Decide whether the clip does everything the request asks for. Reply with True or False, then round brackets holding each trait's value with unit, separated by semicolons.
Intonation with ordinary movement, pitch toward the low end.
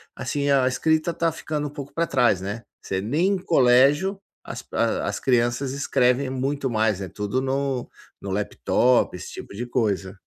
True (4.2 semitones; 130 Hz)